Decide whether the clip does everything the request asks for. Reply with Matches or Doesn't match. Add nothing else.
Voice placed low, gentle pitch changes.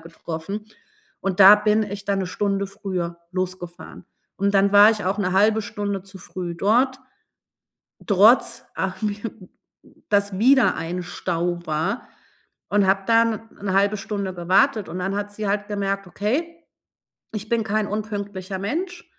Doesn't match